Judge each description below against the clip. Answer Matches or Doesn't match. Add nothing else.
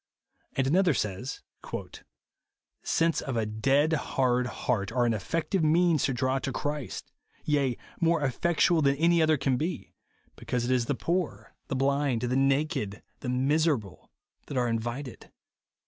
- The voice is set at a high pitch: Doesn't match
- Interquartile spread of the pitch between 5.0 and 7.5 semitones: Doesn't match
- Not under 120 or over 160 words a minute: Matches